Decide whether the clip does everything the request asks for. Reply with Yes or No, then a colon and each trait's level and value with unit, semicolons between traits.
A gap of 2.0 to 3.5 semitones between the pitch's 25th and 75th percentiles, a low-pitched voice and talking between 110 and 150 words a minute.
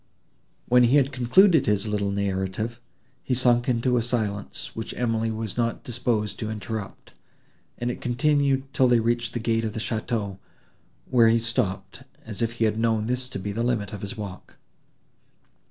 No: narrow, 2.5 semitones; low, 115 Hz; average, 175 wpm